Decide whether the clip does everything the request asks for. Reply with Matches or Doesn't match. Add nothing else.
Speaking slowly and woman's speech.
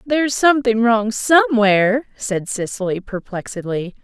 Matches